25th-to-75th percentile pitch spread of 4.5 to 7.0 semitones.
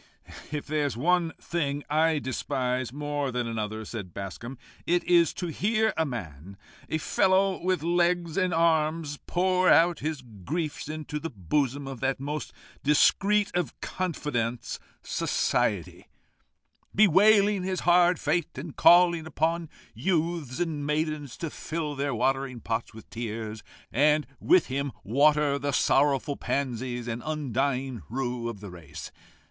Yes: average, 5.2 semitones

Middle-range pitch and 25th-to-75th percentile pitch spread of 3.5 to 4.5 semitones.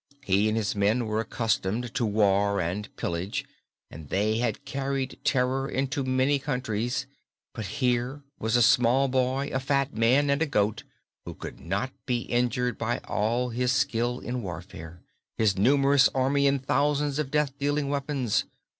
No: low, 125 Hz; average, 4.1 semitones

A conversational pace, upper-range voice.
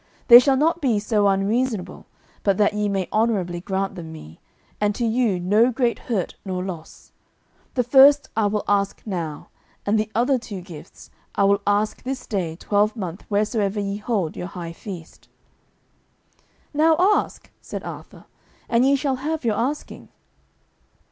Yes: average, 155 wpm; high, 210 Hz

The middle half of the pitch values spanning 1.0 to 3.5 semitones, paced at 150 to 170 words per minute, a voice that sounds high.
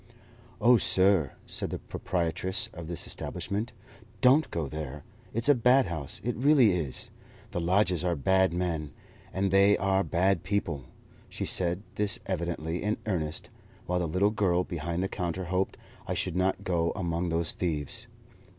No: average, 2.9 semitones; average, 160 wpm; very low, 90 Hz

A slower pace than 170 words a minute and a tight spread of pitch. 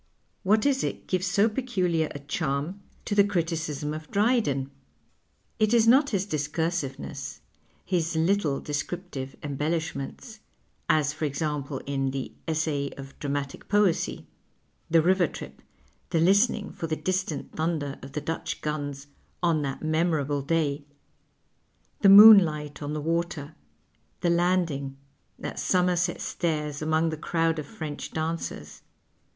No: average, 145 wpm; average, 3.9 semitones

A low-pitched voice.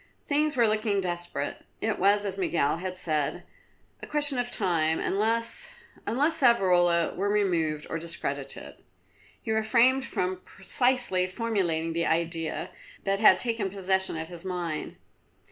No: high, 190 Hz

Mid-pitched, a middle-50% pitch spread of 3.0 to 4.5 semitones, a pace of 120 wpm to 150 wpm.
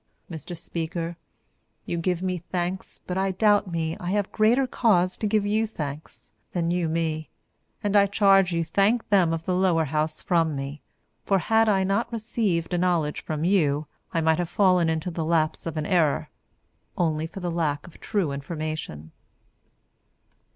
No: medium, 175 Hz; average, 3.4 semitones; average, 170 wpm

